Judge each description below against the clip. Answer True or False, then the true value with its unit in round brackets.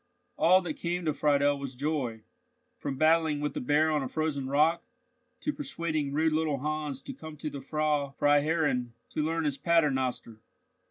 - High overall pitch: False (150 Hz)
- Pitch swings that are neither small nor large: False (2.3 semitones)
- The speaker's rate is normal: True (170 wpm)